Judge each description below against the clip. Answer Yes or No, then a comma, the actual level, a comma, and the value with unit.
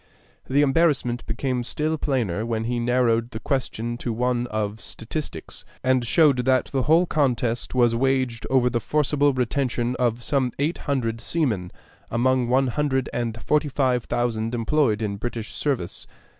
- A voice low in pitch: Yes, low, 125 Hz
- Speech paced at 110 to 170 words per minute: Yes, average, 155 wpm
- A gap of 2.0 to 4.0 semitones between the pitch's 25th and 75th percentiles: Yes, average, 2.8 semitones